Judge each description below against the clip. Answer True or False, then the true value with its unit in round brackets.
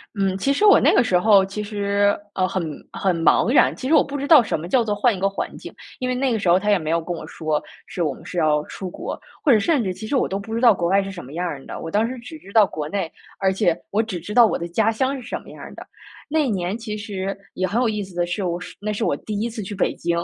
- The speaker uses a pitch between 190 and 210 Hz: True (200 Hz)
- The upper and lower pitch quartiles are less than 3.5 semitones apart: False (4.0 semitones)